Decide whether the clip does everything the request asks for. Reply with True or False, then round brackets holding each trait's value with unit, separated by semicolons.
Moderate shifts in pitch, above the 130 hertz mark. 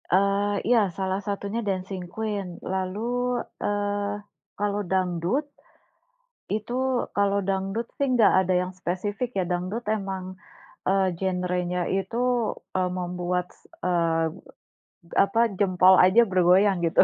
False (2.0 semitones; 190 Hz)